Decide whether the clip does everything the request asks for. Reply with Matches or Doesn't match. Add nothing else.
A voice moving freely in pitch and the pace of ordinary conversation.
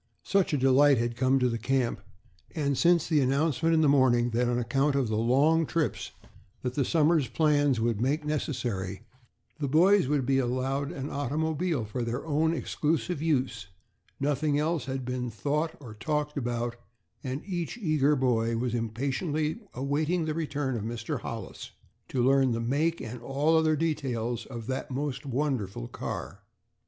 Doesn't match